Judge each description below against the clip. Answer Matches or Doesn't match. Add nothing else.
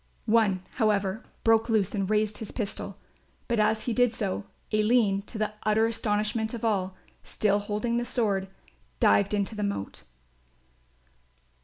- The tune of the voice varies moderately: Doesn't match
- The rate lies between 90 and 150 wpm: Matches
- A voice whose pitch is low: Doesn't match